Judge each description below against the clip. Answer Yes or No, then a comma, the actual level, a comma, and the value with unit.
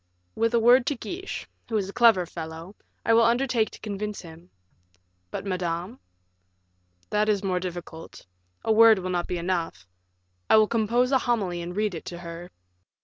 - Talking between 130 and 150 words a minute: No, average, 175 wpm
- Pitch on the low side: No, high, 200 Hz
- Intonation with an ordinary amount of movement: Yes, average, 4.5 semitones